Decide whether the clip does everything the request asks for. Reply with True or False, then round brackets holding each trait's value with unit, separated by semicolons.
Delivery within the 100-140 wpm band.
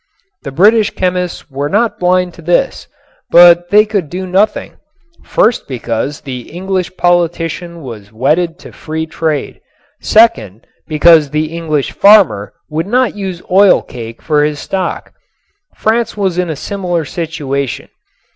True (135 wpm)